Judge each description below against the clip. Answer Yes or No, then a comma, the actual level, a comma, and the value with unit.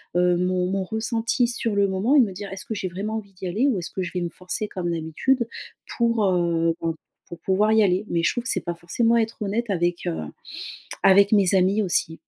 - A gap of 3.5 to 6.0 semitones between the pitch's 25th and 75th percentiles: Yes, average, 3.8 semitones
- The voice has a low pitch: No, high, 195 Hz